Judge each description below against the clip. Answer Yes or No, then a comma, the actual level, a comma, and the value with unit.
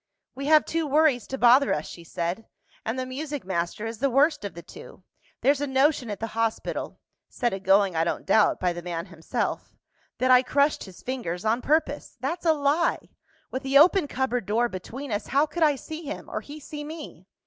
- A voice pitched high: Yes, very high, 255 Hz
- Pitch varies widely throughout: Yes, wide, 6.0 semitones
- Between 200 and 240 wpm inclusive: Yes, fast, 205 wpm